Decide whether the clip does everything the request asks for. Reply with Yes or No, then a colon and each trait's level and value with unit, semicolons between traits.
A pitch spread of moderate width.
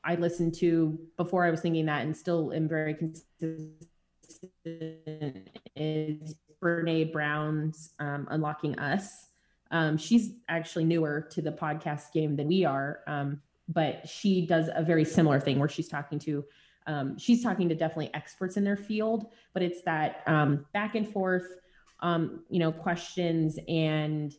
No: narrow, 2.3 semitones